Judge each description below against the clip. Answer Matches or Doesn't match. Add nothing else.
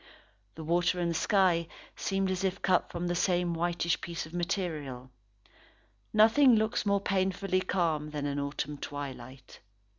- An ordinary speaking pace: Matches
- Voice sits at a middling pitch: Matches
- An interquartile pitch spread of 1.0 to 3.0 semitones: Doesn't match